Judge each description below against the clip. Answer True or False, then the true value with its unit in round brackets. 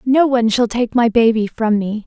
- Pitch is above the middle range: True (230 Hz)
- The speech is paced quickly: True (235 wpm)